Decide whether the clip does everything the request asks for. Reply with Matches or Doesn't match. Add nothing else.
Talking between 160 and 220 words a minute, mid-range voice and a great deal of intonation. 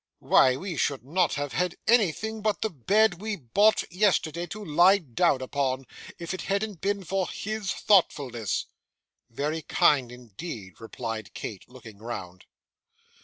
Doesn't match